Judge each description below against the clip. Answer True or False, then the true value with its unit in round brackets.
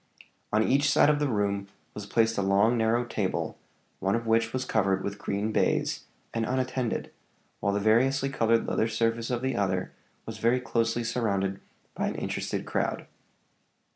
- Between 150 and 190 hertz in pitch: False (115 Hz)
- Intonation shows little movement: False (3.2 semitones)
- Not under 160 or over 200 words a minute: True (170 wpm)